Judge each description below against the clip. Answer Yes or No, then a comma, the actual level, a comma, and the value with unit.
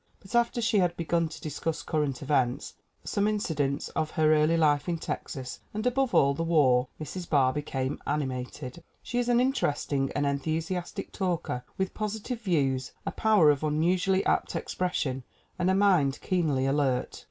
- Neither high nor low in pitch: Yes, medium, 155 Hz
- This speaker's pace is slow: No, average, 165 wpm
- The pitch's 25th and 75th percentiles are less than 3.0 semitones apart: No, average, 5.2 semitones